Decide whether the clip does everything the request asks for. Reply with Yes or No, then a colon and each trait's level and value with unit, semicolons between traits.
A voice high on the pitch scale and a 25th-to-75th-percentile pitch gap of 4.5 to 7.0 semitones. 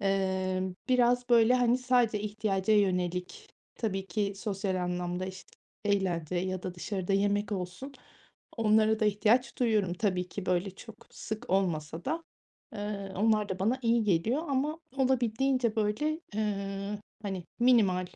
No: high, 205 Hz; average, 3.8 semitones